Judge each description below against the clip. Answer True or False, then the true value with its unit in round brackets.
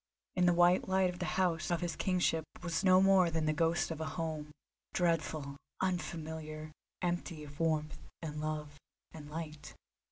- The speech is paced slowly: False (160 wpm)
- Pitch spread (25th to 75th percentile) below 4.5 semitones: True (2.4 semitones)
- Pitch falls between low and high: True (165 Hz)